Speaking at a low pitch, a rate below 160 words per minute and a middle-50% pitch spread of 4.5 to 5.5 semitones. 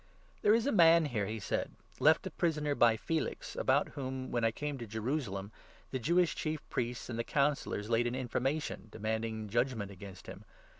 No: low, 125 Hz; average, 185 wpm; average, 5.1 semitones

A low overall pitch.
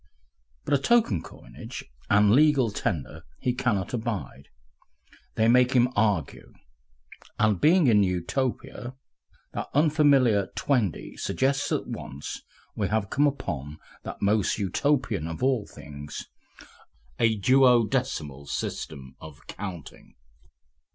Yes: low, 110 Hz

